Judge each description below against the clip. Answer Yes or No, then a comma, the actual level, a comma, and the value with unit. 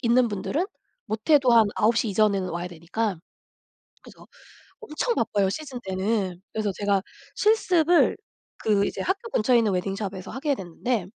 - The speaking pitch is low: No, high, 215 Hz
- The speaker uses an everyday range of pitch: Yes, average, 4.9 semitones